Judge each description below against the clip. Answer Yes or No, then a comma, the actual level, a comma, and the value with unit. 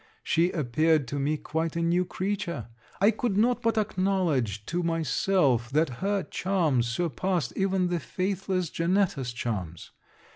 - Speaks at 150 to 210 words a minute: No, average, 140 wpm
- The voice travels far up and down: Yes, wide, 5.8 semitones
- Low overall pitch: No, medium, 170 Hz